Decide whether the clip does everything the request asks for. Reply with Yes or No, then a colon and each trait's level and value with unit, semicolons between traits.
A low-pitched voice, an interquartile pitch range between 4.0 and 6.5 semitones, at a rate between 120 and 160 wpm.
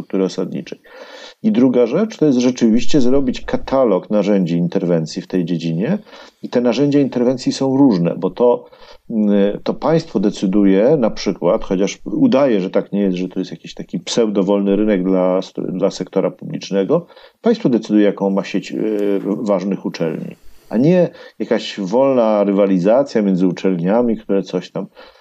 Yes: low, 100 Hz; average, 5.1 semitones; average, 150 wpm